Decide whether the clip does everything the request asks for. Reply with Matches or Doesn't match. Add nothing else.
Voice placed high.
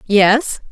Matches